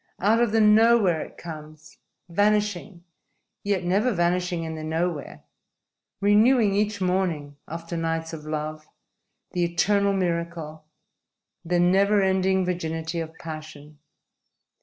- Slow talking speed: Yes, slow, 115 wpm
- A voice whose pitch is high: No, medium, 175 Hz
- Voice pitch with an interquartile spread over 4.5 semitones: No, average, 3.8 semitones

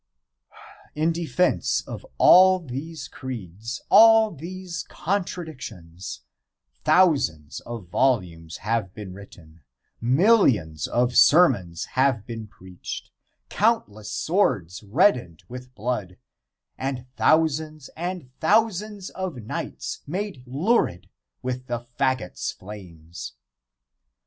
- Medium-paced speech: No, slow, 95 wpm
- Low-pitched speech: Yes, low, 130 Hz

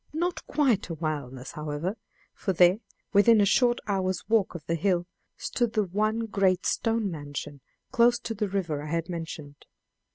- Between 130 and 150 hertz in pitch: No, high, 190 Hz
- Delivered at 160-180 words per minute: Yes, average, 165 wpm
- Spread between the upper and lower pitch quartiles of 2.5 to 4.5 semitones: No, wide, 5.4 semitones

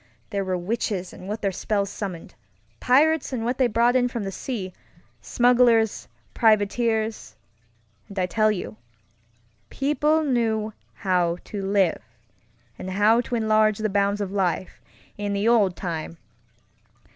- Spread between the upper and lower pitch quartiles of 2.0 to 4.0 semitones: Yes, average, 3.7 semitones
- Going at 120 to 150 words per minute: Yes, slow, 135 wpm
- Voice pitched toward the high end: Yes, high, 210 Hz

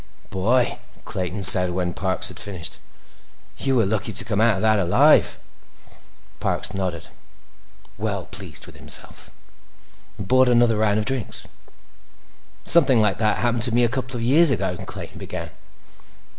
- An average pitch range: Yes, average, 4.2 semitones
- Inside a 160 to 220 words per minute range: No, average, 150 wpm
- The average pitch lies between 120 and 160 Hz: No, low, 110 Hz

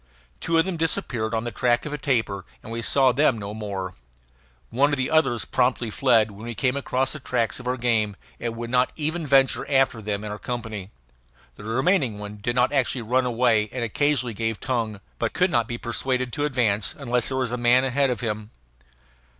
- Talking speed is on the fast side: Yes, fast, 210 wpm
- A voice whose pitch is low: Yes, low, 120 Hz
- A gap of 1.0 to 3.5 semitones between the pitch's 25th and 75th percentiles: Yes, average, 3.1 semitones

